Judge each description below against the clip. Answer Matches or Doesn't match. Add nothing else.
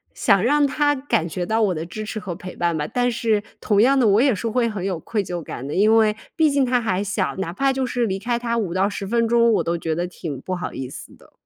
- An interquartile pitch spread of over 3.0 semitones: Matches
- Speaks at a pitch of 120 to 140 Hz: Doesn't match